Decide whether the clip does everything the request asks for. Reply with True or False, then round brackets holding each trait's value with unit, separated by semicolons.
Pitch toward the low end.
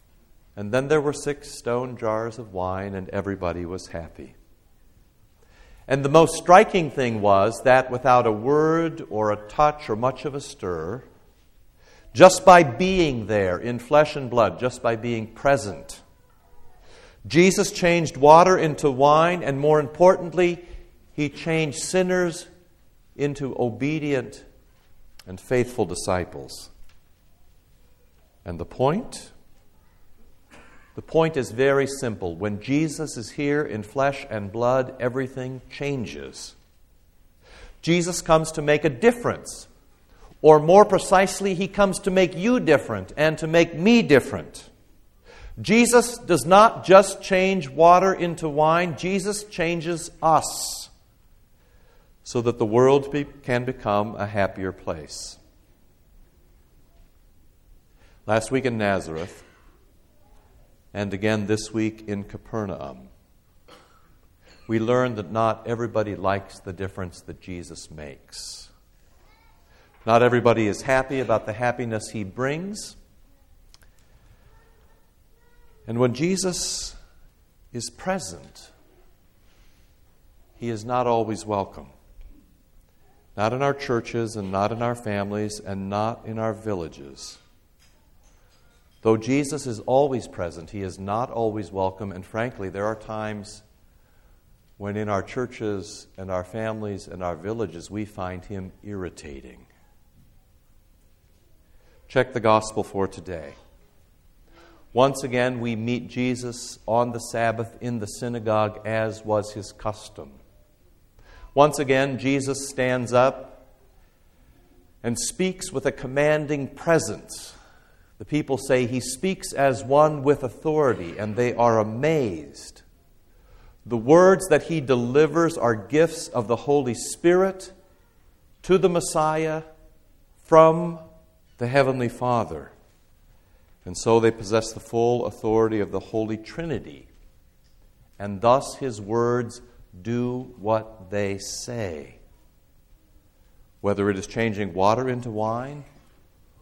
True (115 Hz)